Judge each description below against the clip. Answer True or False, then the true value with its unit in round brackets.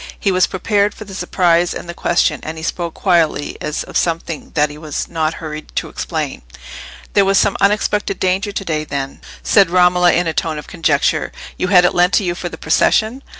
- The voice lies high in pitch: False (175 Hz)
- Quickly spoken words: True (210 wpm)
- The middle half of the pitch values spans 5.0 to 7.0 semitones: False (3.5 semitones)